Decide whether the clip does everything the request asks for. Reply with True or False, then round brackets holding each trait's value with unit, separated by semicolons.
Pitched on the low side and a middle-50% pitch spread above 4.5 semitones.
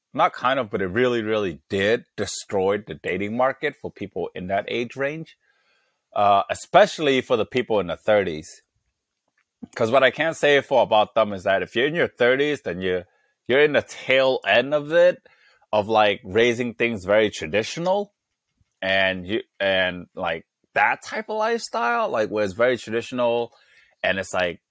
True (120 Hz; 5.6 semitones)